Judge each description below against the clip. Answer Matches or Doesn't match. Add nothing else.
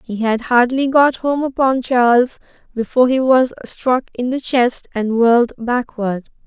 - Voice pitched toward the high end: Matches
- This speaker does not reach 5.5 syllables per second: Matches